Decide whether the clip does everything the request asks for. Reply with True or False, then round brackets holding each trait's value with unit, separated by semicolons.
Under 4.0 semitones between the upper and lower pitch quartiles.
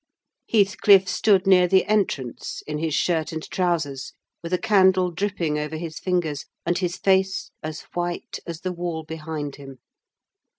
True (3.2 semitones)